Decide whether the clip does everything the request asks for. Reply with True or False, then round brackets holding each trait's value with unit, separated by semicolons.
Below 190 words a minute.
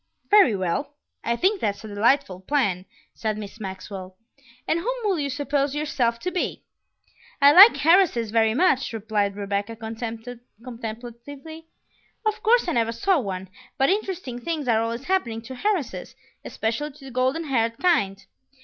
True (150 wpm)